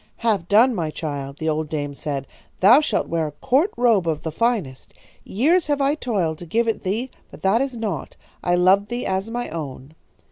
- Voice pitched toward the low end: No, high, 190 Hz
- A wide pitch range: Yes, wide, 7.3 semitones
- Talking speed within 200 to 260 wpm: Yes, fast, 205 wpm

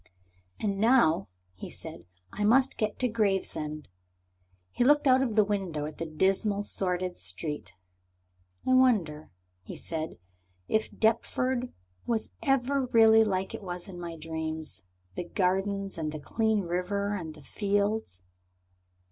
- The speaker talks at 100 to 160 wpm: Yes, average, 140 wpm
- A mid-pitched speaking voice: No, high, 200 Hz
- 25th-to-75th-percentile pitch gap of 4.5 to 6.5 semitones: Yes, average, 5.2 semitones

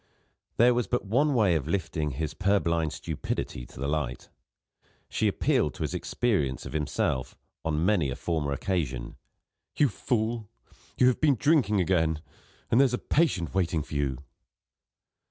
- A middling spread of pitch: No, wide, 7.4 semitones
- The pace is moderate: Yes, average, 155 wpm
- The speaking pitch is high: No, very low, 85 Hz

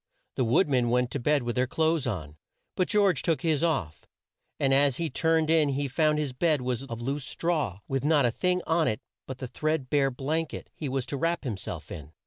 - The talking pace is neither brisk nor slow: No, fast, 230 wpm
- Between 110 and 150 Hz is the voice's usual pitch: Yes, medium, 140 Hz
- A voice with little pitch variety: No, average, 4.3 semitones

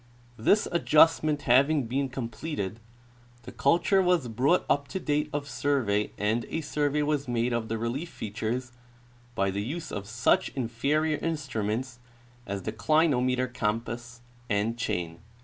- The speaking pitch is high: No, low, 125 Hz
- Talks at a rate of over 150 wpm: No, average, 140 wpm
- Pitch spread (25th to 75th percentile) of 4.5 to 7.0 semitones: Yes, average, 4.8 semitones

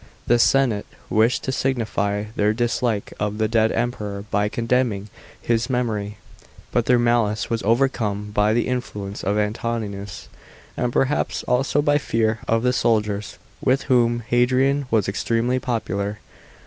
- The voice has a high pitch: No, low, 115 Hz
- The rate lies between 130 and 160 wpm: Yes, average, 140 wpm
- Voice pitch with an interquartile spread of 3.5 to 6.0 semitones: No, average, 3.0 semitones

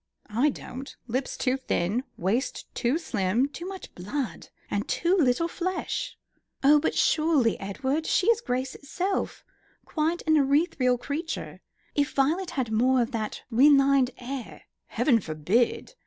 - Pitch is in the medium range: No, very high, 270 Hz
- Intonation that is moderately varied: Yes, average, 4.6 semitones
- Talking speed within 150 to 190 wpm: No, average, 140 wpm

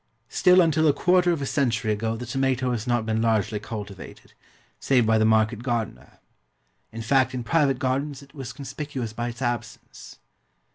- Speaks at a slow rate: No, average, 175 wpm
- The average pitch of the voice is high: No, low, 120 Hz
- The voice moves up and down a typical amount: Yes, average, 3.6 semitones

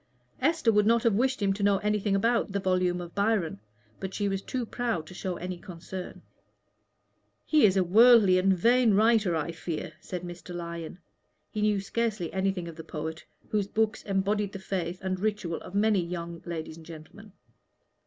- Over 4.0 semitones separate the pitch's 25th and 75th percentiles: No, average, 3.4 semitones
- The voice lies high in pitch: Yes, high, 195 Hz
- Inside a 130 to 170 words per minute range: No, average, 185 wpm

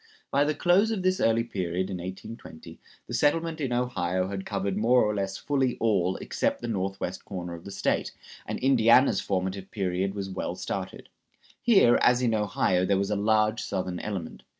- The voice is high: No, low, 100 Hz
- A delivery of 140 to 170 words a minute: No, average, 180 wpm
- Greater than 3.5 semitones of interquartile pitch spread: Yes, average, 4.6 semitones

